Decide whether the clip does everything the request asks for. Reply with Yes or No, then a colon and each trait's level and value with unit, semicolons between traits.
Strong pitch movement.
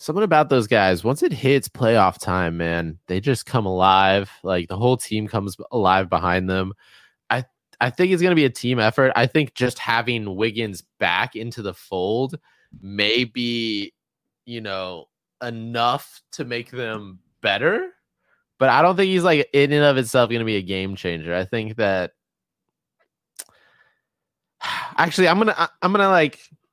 Yes: wide, 6.4 semitones